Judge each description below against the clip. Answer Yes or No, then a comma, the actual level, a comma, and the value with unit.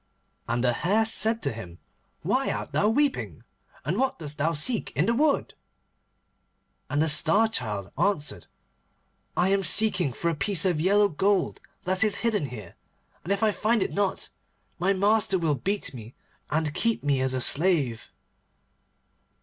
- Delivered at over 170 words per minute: No, average, 165 wpm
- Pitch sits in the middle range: Yes, medium, 180 Hz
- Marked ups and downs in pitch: Yes, wide, 6.4 semitones